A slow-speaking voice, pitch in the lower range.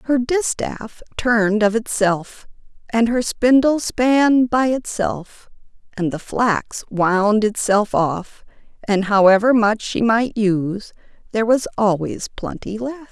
No: slow, 130 wpm; high, 220 Hz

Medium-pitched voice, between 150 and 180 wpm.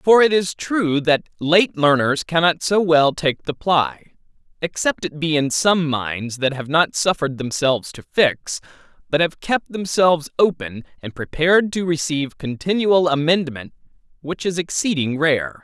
Yes: medium, 155 Hz; average, 155 wpm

